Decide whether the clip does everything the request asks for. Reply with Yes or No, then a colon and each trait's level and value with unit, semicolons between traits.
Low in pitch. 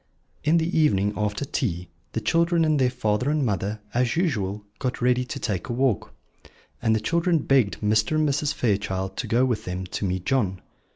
Yes: low, 120 Hz